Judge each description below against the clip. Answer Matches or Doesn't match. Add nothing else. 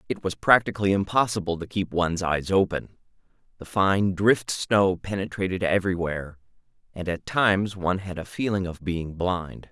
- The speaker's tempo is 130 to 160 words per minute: Matches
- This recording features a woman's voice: Doesn't match